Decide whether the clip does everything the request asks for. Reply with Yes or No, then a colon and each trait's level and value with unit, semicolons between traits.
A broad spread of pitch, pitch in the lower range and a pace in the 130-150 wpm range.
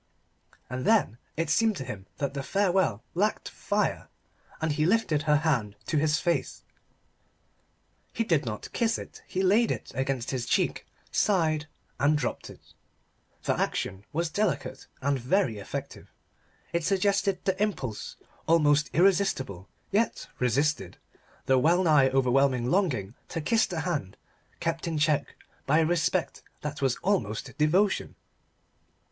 No: wide, 5.8 semitones; medium, 155 Hz; average, 140 wpm